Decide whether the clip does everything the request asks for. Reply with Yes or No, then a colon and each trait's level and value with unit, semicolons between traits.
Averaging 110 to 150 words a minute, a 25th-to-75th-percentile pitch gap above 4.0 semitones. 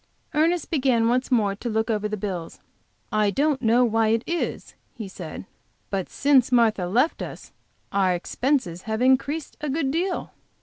No: average, 165 wpm; average, 4.8 semitones